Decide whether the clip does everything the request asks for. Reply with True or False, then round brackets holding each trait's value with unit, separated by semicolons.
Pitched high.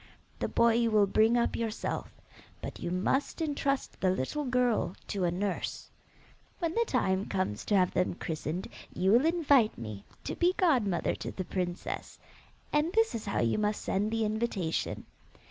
True (215 Hz)